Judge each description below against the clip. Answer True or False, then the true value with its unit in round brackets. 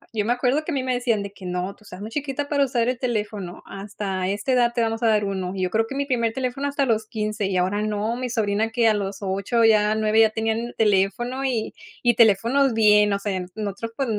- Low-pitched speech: False (220 Hz)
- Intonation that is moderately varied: True (3.2 semitones)